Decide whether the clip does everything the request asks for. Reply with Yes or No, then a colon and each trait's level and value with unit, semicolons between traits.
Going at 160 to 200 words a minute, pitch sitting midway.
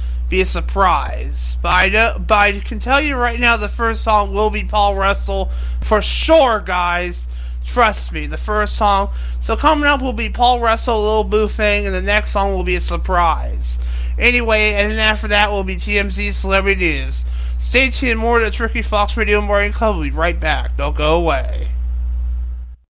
No: average, 190 wpm; high, 195 Hz